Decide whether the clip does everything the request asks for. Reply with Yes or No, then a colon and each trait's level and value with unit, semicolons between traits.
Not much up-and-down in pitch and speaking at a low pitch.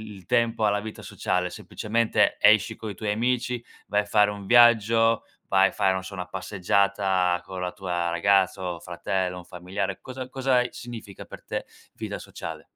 No: average, 3.6 semitones; low, 100 Hz